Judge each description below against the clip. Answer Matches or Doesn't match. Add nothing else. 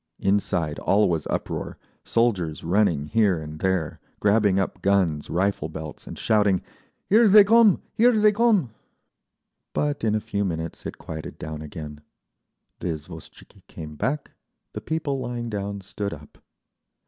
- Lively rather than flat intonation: Matches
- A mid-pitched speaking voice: Doesn't match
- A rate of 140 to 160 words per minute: Matches